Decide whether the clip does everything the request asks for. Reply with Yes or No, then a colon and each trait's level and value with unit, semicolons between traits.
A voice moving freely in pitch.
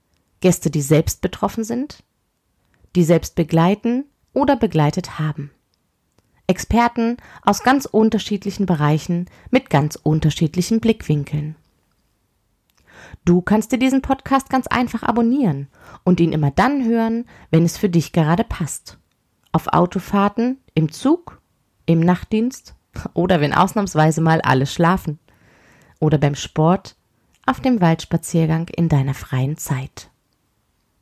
Yes: wide, 6.9 semitones